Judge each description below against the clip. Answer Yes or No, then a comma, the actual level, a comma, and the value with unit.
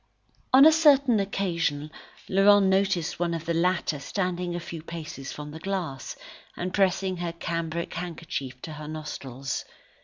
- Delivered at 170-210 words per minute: No, average, 155 wpm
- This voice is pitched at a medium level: Yes, medium, 170 Hz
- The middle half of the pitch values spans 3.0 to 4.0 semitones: Yes, average, 3.6 semitones